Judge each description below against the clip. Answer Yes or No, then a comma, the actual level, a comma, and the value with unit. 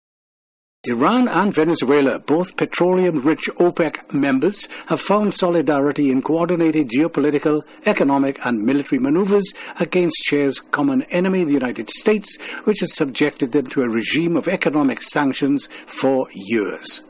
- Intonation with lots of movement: No, average, 4.9 semitones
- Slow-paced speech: Yes, slow, 125 wpm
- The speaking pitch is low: No, medium, 165 Hz